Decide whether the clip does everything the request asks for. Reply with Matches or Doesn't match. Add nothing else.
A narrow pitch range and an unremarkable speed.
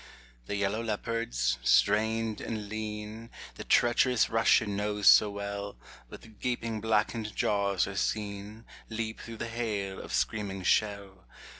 Doesn't match